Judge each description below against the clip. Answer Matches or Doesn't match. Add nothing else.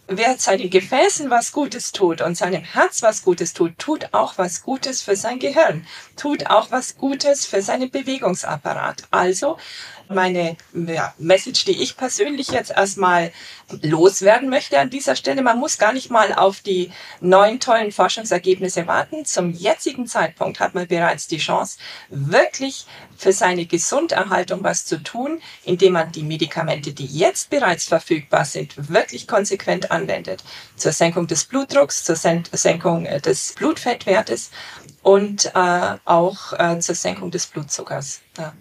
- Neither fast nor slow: Matches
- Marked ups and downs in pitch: Matches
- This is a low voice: Doesn't match